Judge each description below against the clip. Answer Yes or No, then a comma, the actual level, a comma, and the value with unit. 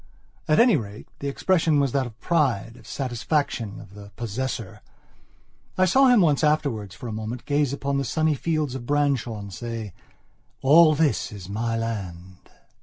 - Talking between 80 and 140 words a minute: No, average, 170 wpm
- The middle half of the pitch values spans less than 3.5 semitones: No, wide, 5.5 semitones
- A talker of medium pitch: No, low, 130 Hz